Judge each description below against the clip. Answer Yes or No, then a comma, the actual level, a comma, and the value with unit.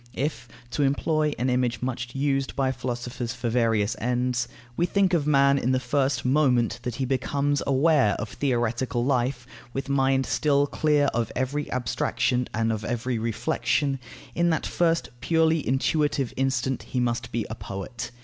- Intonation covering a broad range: No, average, 2.8 semitones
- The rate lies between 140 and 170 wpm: Yes, average, 160 wpm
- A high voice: No, low, 130 Hz